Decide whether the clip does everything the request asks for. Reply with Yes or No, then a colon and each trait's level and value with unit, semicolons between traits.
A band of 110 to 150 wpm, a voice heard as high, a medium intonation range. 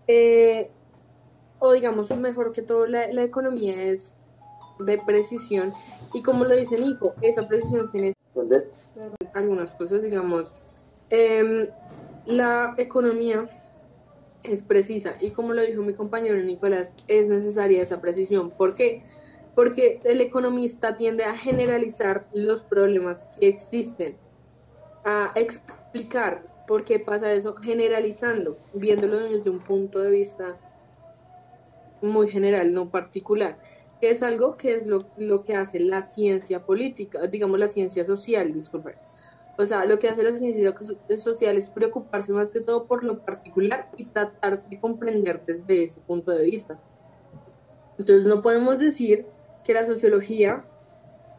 Yes: slow, 135 wpm; high, 210 Hz; average, 3.2 semitones